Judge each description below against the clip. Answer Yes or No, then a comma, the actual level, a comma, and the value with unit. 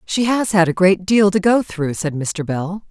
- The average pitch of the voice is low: No, medium, 185 Hz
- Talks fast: Yes, fast, 250 wpm